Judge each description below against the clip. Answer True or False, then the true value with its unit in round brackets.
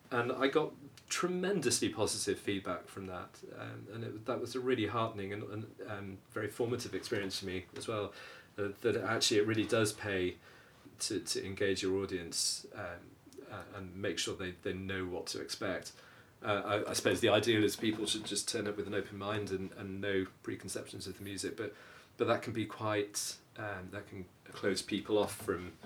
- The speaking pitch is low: True (100 Hz)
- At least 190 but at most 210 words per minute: True (200 wpm)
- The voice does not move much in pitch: True (2.2 semitones)